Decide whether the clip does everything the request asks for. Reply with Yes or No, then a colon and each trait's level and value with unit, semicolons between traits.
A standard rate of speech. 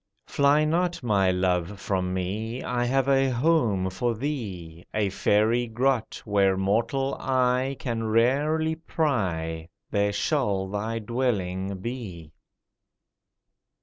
No: slow, 115 wpm